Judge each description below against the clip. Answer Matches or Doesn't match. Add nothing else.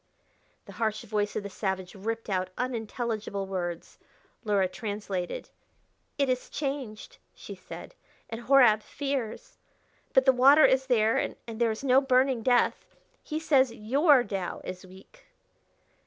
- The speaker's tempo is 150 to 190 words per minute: Doesn't match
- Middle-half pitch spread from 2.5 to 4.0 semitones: Doesn't match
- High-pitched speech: Matches